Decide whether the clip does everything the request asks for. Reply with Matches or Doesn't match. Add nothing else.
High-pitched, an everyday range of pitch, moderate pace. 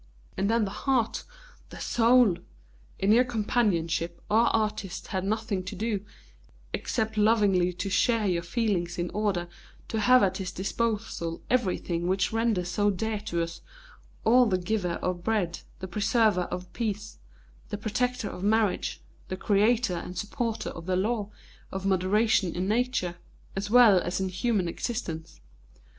Matches